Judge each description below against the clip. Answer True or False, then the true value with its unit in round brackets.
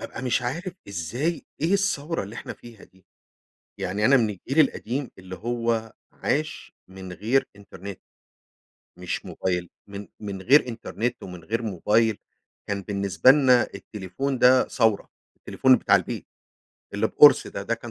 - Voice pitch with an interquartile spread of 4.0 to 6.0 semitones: True (4.8 semitones)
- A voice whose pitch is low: True (115 Hz)